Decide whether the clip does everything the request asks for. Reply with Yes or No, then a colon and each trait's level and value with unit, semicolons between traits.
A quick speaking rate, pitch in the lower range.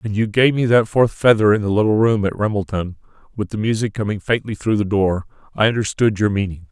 Yes: fast, 225 wpm; low, 105 Hz